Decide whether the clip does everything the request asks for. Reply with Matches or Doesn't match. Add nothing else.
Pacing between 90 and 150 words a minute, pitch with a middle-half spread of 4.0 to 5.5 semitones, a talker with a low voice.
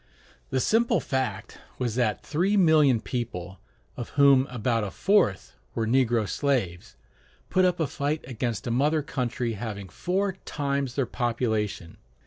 Matches